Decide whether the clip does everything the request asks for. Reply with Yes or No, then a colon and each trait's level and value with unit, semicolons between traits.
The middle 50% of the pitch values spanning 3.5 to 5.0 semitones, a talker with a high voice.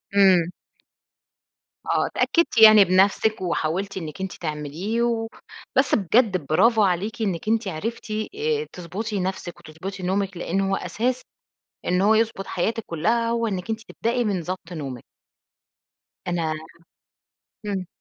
Yes: average, 4.1 semitones; high, 195 Hz